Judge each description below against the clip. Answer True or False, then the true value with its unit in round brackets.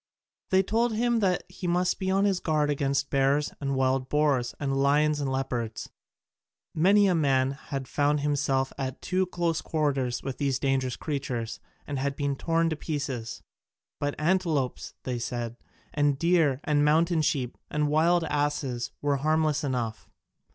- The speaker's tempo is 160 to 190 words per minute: False (150 wpm)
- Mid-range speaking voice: True (145 Hz)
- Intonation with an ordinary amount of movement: True (3.2 semitones)